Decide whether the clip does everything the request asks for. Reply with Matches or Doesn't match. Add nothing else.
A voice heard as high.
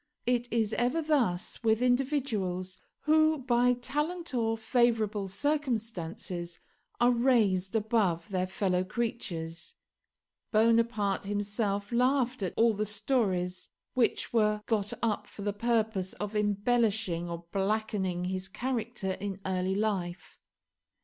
Matches